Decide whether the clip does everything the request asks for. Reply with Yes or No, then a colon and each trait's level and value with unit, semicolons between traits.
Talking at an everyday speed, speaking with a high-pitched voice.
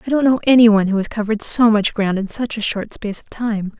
No: fast, 285 wpm; high, 220 Hz